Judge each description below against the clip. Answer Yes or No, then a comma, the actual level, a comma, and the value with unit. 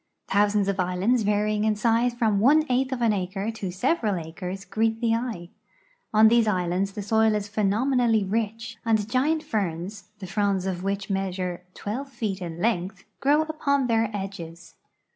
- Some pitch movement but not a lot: Yes, average, 3.0 semitones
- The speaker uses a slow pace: No, average, 165 wpm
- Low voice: No, high, 210 Hz